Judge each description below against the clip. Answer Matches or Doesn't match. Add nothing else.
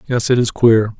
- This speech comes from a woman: Doesn't match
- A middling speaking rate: Doesn't match